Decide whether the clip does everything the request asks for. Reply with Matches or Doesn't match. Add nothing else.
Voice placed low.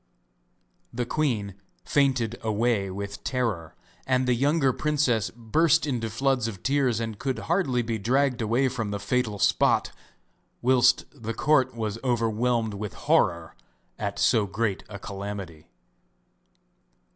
Matches